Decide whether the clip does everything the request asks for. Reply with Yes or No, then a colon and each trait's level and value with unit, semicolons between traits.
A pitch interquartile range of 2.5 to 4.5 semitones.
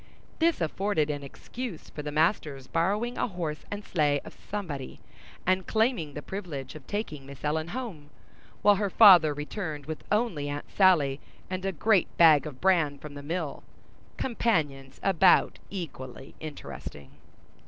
No: average, 5.3 semitones